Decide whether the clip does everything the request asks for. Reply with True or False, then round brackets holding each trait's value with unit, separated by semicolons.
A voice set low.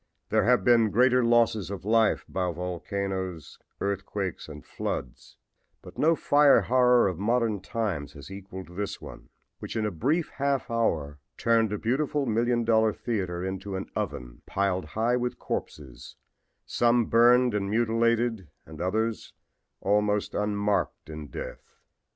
True (105 Hz)